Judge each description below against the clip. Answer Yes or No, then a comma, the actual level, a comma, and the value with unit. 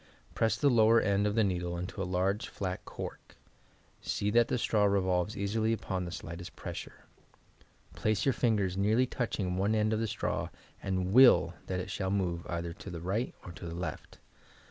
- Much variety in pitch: No, average, 3.3 semitones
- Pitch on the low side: Yes, low, 100 Hz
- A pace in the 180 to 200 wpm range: Yes, average, 190 wpm